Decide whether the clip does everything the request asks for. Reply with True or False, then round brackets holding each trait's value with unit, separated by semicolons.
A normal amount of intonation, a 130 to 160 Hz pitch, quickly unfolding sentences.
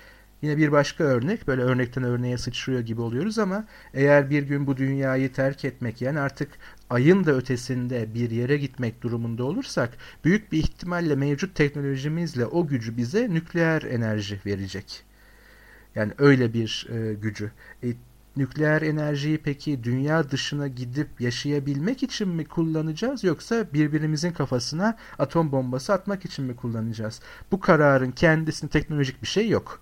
True (4.3 semitones; 140 Hz; 145 wpm)